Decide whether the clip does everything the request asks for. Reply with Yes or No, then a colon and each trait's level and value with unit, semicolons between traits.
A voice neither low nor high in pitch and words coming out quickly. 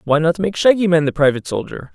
Yes: medium, 170 Hz; fast, 245 wpm